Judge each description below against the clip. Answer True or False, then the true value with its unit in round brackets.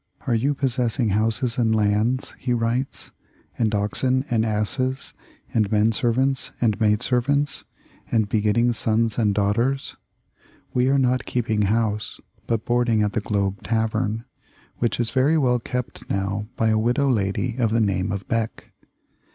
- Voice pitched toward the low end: True (115 Hz)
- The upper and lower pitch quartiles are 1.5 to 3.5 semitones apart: True (2.8 semitones)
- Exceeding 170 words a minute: False (155 wpm)